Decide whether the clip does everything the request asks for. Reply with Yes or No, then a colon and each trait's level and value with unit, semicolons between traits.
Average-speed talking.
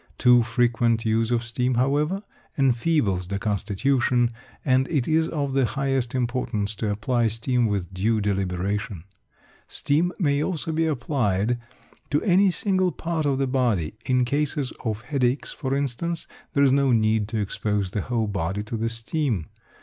Yes: average, 155 wpm